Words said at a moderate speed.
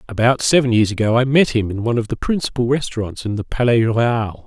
No: fast, 230 wpm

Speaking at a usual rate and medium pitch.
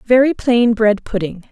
No: average, 160 wpm; high, 225 Hz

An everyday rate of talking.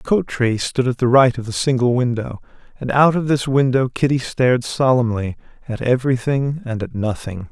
Yes: average, 190 wpm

